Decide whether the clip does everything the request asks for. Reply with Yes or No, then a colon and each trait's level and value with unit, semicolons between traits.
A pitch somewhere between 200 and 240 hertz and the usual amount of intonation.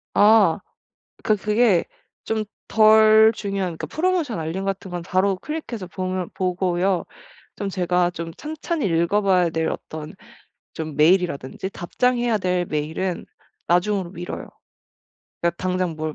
No: medium, 185 Hz; average, 3.6 semitones